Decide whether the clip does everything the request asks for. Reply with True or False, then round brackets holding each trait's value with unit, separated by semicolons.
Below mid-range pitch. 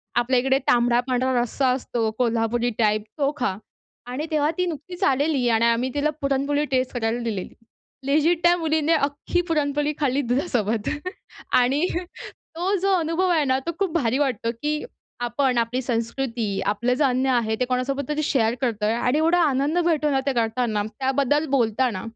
False (260 Hz)